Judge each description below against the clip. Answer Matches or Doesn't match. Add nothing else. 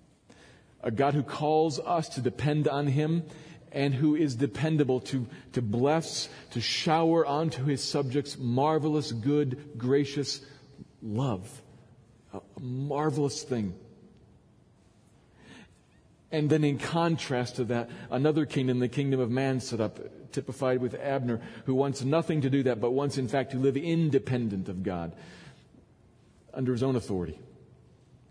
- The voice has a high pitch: Doesn't match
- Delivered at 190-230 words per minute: Doesn't match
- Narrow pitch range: Doesn't match